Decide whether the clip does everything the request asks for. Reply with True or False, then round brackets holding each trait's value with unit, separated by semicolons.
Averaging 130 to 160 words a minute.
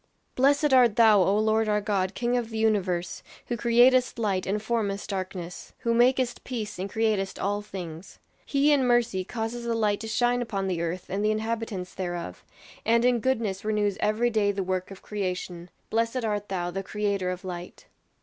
False (185 wpm)